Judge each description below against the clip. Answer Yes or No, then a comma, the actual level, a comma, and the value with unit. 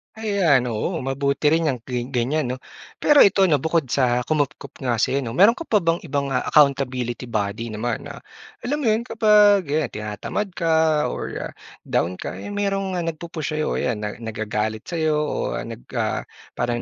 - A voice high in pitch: No, medium, 145 Hz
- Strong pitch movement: Yes, wide, 6.2 semitones